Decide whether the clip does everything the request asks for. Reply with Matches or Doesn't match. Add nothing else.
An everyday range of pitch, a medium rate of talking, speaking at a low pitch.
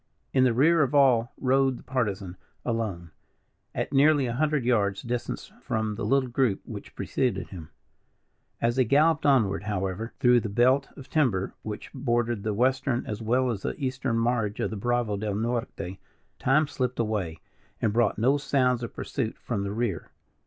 Matches